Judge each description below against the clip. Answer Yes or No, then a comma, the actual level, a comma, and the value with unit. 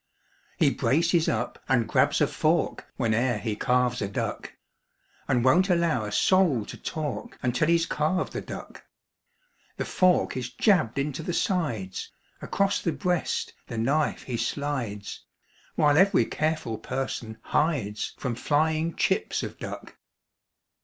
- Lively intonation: Yes, wide, 5.8 semitones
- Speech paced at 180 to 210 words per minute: No, average, 140 wpm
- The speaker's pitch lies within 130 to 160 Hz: Yes, medium, 140 Hz